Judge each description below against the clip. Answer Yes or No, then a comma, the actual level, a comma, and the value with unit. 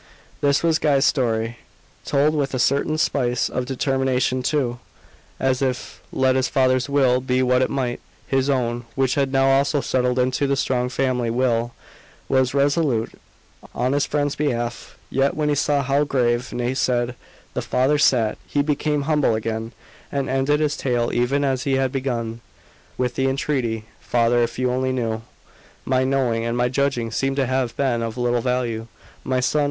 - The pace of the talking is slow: No, average, 175 wpm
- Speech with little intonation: Yes, narrow, 2.3 semitones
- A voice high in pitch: No, low, 130 Hz